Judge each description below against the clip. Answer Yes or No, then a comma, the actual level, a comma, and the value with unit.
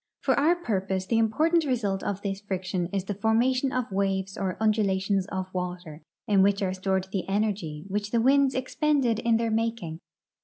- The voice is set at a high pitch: Yes, high, 200 Hz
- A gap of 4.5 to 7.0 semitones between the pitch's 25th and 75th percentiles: No, average, 3.4 semitones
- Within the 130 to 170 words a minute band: No, average, 180 wpm